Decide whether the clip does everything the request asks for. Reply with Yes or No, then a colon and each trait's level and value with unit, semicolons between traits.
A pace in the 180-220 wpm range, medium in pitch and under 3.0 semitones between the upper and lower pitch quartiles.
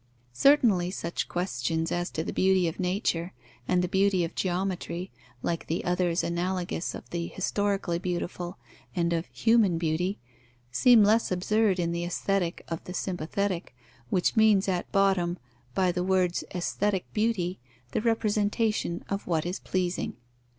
No: average, 145 wpm; medium, 180 Hz; narrow, 2.4 semitones